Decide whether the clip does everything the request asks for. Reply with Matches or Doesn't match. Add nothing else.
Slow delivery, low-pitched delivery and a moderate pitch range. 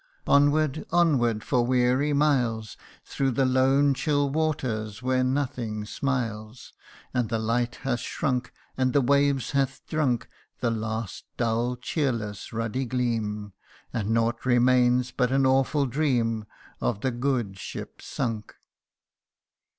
Matches